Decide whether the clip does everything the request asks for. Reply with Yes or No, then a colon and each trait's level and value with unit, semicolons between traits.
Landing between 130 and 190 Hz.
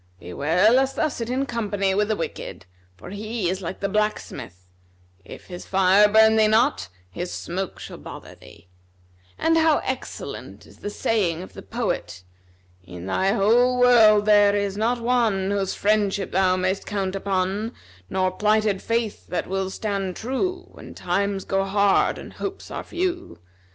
No: high, 200 Hz